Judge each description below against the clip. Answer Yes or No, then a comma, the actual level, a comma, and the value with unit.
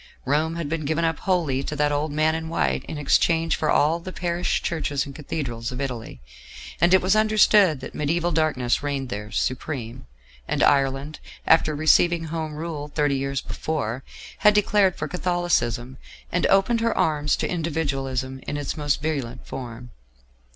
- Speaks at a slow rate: No, average, 165 wpm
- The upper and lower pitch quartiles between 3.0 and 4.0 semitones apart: Yes, average, 3.6 semitones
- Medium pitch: Yes, medium, 150 Hz